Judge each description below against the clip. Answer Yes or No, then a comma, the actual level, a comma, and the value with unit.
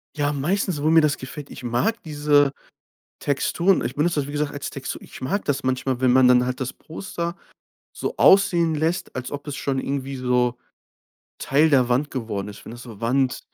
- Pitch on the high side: No, medium, 140 Hz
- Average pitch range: Yes, average, 3.3 semitones